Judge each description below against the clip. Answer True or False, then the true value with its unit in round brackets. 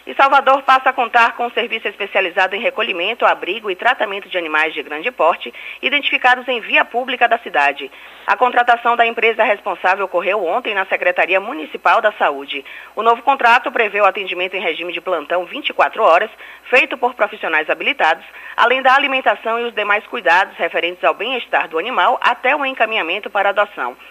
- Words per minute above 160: True (175 wpm)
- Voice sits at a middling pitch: False (220 Hz)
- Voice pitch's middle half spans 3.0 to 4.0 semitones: False (4.7 semitones)